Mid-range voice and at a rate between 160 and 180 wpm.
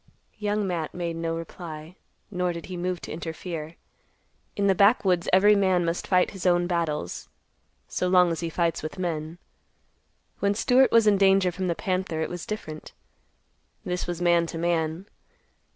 Yes: medium, 175 Hz; average, 170 wpm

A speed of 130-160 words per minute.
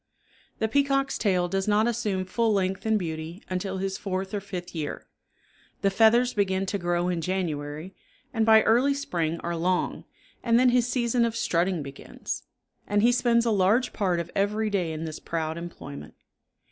No: average, 175 wpm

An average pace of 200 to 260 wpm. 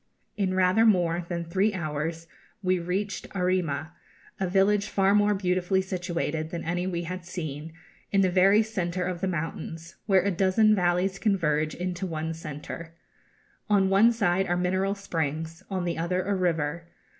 No: average, 160 wpm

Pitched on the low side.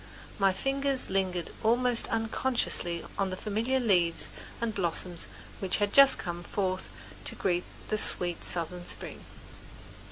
No: high, 195 Hz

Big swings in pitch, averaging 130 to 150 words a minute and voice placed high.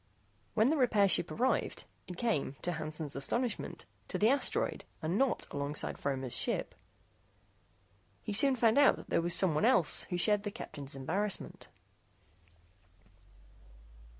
Yes: wide, 7.4 semitones; slow, 135 wpm; high, 195 Hz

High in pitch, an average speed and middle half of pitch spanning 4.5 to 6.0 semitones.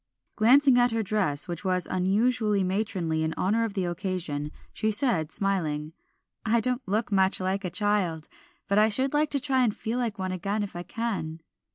No: high, 200 Hz; average, 190 wpm; average, 3.9 semitones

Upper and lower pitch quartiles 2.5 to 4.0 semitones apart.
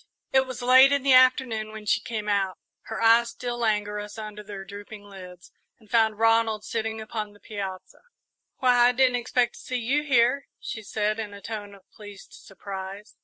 Yes: average, 2.9 semitones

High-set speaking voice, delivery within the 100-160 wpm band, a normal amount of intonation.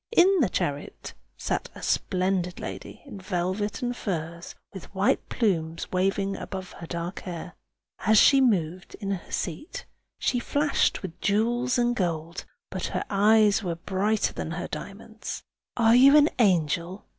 Yes: high, 195 Hz; average, 150 wpm; average, 4.5 semitones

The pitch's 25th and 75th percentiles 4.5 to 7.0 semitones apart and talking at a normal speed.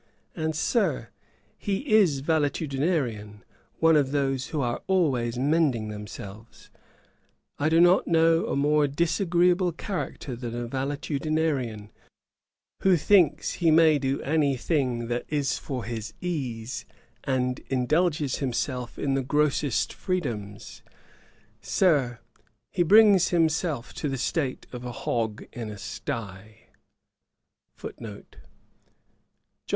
No: average, 5.1 semitones; slow, 115 wpm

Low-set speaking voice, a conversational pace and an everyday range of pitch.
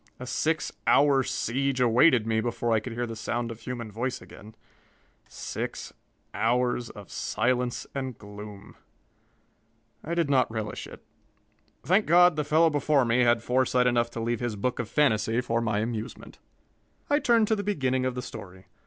Yes: low, 125 Hz; average, 170 wpm; average, 3.4 semitones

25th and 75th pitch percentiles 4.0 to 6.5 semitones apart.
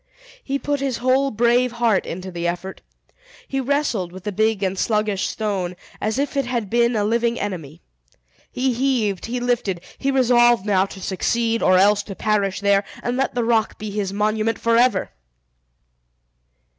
No: average, 3.6 semitones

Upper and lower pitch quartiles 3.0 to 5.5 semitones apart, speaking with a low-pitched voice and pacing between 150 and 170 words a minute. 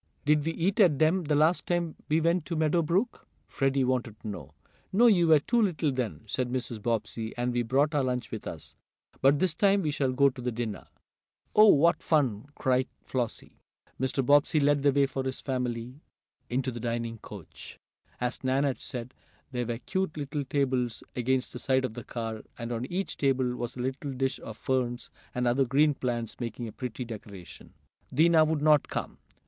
No: average, 3.8 semitones; low, 130 Hz; average, 195 wpm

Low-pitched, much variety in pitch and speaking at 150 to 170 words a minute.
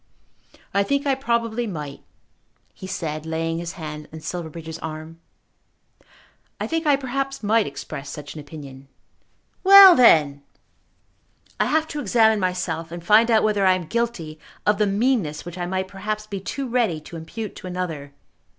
No: medium, 185 Hz; wide, 6.4 semitones; average, 160 wpm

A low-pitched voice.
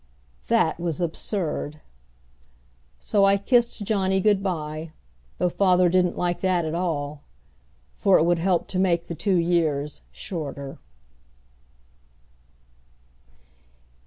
No: medium, 175 Hz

